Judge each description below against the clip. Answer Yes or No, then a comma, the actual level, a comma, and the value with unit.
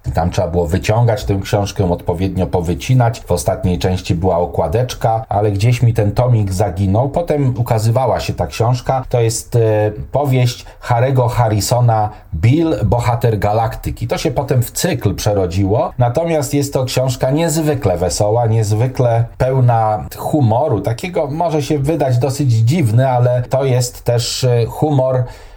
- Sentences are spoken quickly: No, average, 140 wpm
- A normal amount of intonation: Yes, average, 3.8 semitones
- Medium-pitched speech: No, low, 115 Hz